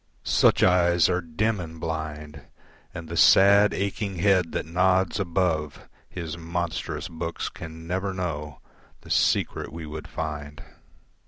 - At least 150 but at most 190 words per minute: No, slow, 135 wpm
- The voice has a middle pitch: No, very low, 85 Hz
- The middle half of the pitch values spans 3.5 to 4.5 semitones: No, average, 2.8 semitones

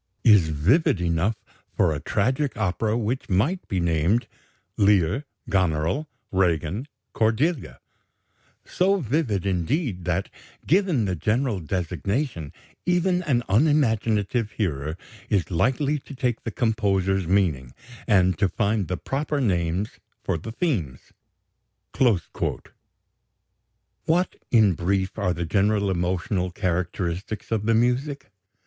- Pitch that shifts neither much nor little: No, wide, 5.8 semitones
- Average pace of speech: No, slow, 115 wpm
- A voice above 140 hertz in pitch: No, low, 100 Hz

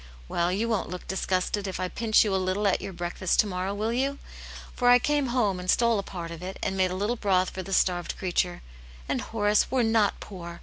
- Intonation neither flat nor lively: Yes, average, 3.4 semitones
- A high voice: Yes, high, 195 Hz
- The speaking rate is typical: No, fast, 235 wpm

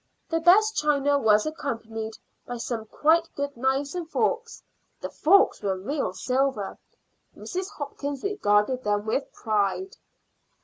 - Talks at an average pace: No, slow, 130 wpm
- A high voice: Yes, very high, 275 Hz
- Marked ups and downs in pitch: Yes, wide, 6.7 semitones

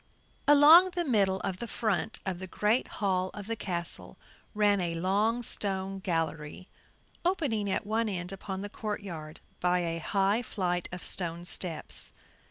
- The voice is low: No, high, 195 Hz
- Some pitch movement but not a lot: Yes, average, 3.4 semitones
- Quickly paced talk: No, average, 160 wpm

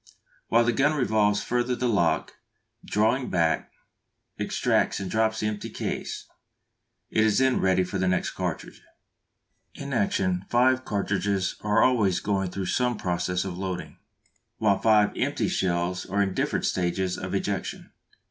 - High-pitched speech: No, low, 100 Hz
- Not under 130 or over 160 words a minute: Yes, average, 150 wpm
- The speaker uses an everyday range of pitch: Yes, average, 3.5 semitones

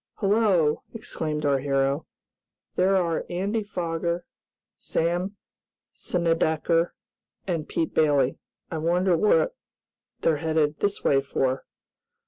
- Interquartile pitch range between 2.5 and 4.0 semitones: Yes, average, 3.2 semitones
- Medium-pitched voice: Yes, medium, 165 Hz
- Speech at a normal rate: No, slow, 105 wpm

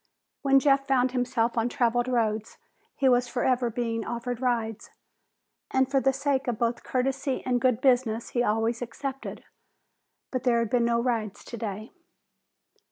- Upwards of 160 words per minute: No, average, 155 wpm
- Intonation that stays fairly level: Yes, narrow, 2.1 semitones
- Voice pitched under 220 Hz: No, high, 245 Hz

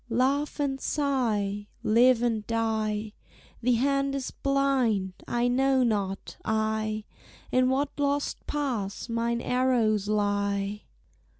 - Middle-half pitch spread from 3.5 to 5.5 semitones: Yes, average, 4.0 semitones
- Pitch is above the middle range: Yes, high, 235 Hz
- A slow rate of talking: Yes, slow, 110 wpm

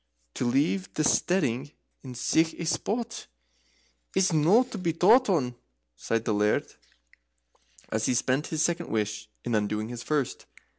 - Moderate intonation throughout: No, wide, 7.1 semitones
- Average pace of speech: Yes, average, 150 wpm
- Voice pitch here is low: No, medium, 145 Hz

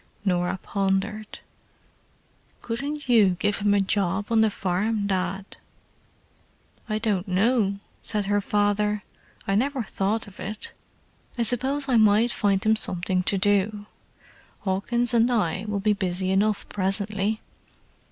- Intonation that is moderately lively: No, narrow, 2.3 semitones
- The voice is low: No, high, 205 Hz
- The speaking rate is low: Yes, slow, 130 wpm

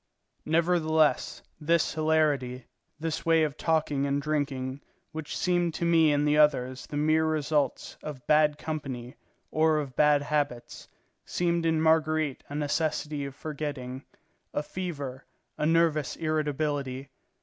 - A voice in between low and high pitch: Yes, medium, 150 Hz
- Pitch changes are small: Yes, narrow, 2.0 semitones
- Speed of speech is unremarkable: No, slow, 130 wpm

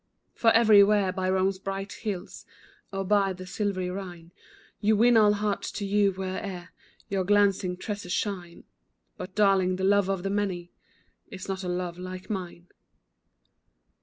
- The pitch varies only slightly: Yes, narrow, 1.7 semitones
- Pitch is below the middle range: No, high, 195 Hz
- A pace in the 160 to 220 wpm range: No, average, 150 wpm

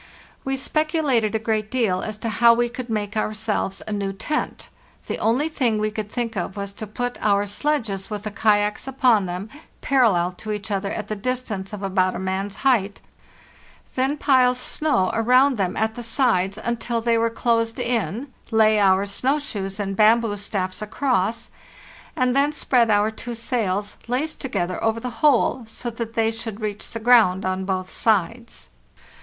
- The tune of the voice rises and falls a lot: No, average, 3.5 semitones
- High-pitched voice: Yes, high, 220 Hz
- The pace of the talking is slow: No, average, 175 wpm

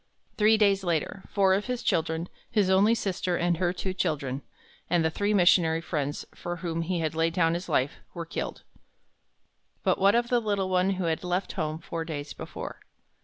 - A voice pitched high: No, medium, 175 Hz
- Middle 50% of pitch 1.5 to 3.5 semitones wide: Yes, average, 3.1 semitones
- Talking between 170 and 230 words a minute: Yes, average, 190 wpm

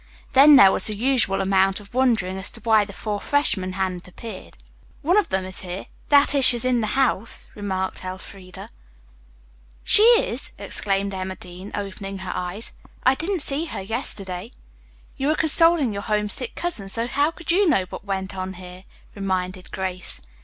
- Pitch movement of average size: No, wide, 5.8 semitones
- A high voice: Yes, high, 200 Hz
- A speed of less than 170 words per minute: No, average, 175 wpm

